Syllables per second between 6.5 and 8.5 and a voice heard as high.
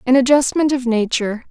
No: 5.9 syllables/s; very high, 255 Hz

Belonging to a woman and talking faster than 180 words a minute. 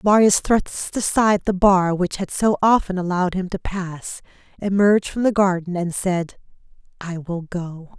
No: female; average, 165 wpm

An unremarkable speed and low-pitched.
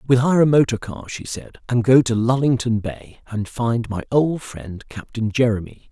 Yes: average, 195 wpm; low, 120 Hz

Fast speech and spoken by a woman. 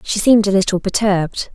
No: average, 195 wpm; female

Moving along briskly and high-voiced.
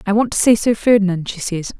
Yes: fast, 270 wpm; high, 205 Hz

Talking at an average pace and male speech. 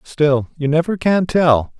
Yes: average, 170 wpm; male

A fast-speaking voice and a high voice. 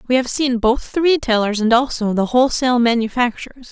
No: average, 175 wpm; high, 245 Hz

